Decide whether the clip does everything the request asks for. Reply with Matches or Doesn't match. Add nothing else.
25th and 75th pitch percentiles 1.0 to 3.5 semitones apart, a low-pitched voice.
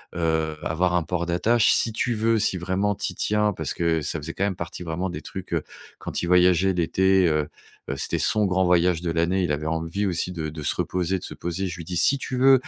Matches